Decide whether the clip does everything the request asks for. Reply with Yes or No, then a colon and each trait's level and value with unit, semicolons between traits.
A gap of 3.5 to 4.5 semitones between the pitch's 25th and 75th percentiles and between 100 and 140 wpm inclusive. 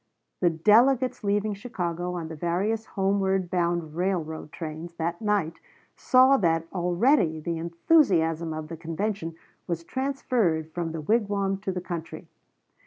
Yes: average, 4.1 semitones; slow, 135 wpm